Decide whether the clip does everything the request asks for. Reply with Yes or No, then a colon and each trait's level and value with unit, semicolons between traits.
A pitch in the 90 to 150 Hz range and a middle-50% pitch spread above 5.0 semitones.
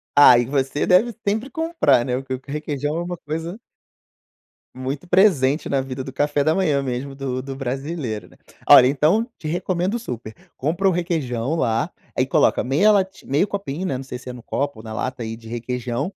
Yes: medium, 140 Hz; wide, 5.4 semitones